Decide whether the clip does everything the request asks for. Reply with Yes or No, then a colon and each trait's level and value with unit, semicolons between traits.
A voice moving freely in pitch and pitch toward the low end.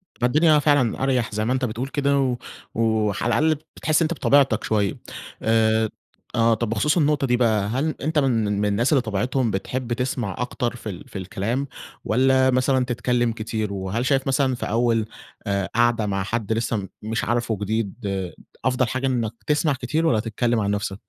No: average, 3.3 semitones; low, 120 Hz